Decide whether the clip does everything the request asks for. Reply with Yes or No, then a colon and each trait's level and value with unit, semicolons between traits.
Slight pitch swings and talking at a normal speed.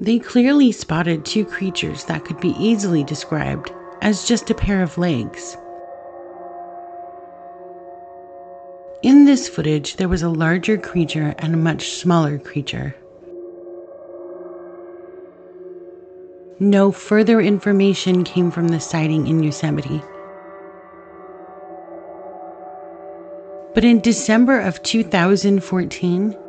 No: narrow, 1.8 semitones; slow, 95 wpm